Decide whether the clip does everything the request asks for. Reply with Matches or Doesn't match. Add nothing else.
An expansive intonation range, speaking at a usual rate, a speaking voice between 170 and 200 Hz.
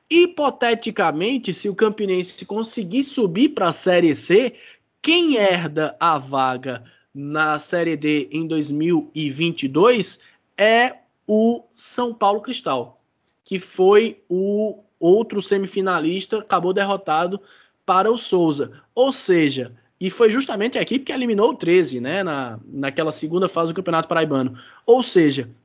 Matches